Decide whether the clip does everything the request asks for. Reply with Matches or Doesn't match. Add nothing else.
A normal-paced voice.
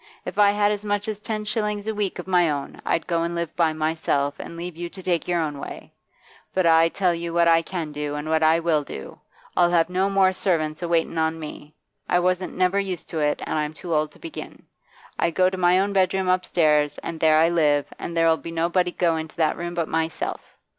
Doesn't match